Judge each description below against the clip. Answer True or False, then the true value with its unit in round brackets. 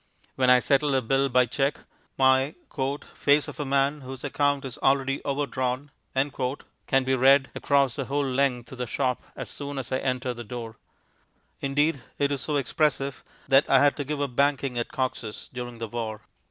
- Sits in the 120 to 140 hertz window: True (135 Hz)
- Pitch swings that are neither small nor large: False (1.9 semitones)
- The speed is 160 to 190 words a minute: True (185 wpm)